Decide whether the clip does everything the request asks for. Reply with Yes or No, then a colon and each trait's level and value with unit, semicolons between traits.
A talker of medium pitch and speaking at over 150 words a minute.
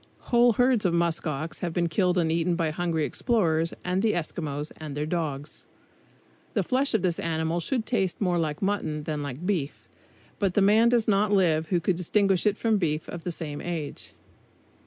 Yes: medium, 175 Hz; average, 190 wpm